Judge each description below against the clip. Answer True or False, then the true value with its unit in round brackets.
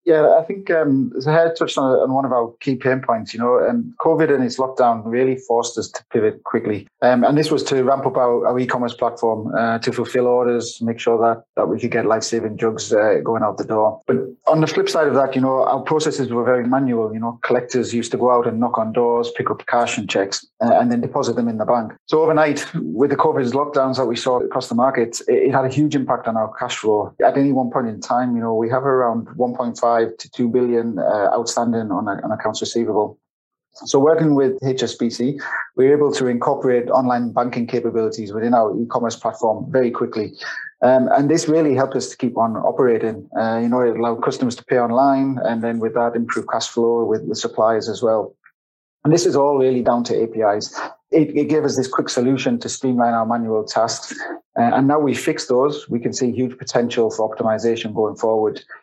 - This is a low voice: True (125 Hz)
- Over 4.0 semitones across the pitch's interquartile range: False (2.7 semitones)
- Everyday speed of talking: False (230 wpm)